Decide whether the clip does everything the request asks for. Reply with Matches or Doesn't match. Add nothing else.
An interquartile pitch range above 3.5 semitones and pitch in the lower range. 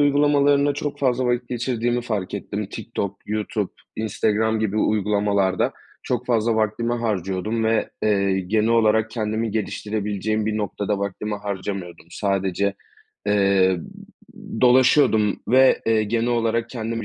Doesn't match